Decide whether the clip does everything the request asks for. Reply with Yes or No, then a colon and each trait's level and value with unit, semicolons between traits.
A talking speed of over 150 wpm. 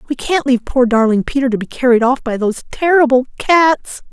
Yes: fast, 205 wpm